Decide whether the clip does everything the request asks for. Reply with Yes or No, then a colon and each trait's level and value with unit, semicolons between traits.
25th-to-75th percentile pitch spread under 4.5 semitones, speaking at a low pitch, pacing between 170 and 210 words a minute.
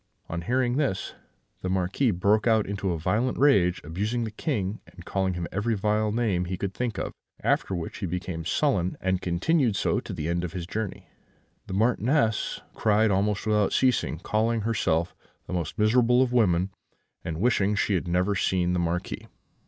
Yes: average, 4.0 semitones; low, 100 Hz; average, 180 wpm